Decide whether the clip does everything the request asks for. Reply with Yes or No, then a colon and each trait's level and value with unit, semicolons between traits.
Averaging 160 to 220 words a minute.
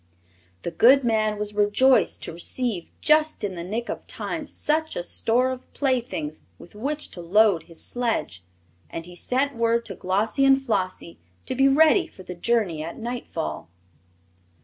Yes: average, 165 wpm